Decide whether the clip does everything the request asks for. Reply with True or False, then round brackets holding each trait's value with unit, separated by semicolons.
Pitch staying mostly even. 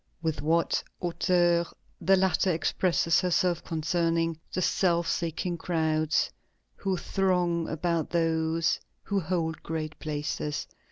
True (1.9 semitones)